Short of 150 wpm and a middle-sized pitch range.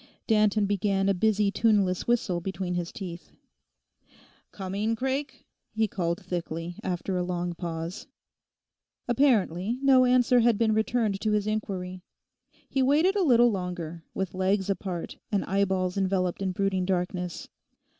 Yes: slow, 135 wpm; average, 3.4 semitones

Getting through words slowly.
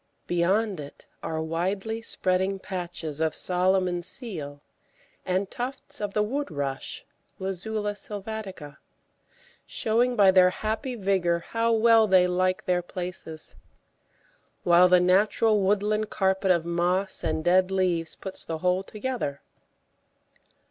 Yes: slow, 120 wpm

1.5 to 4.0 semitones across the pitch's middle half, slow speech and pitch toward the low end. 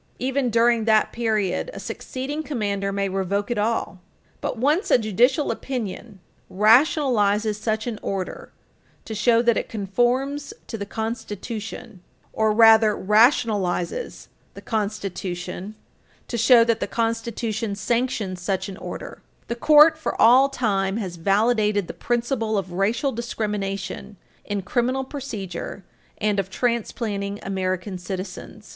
No: average, 3.2 semitones; slow, 130 wpm; high, 220 Hz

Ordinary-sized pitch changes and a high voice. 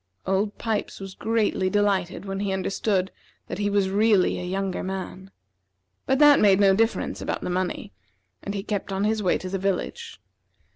No: narrow, 1.5 semitones; high, 195 Hz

